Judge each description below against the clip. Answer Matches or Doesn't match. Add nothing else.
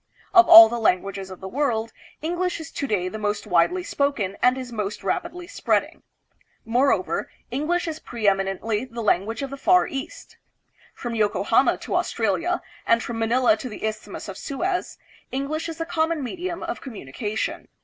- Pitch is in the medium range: Doesn't match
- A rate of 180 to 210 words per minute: Doesn't match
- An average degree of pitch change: Doesn't match